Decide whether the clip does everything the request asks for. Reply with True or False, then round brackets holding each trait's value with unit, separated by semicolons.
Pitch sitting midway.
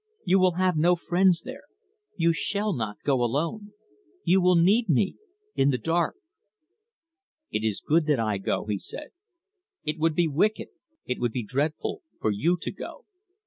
True (165 Hz)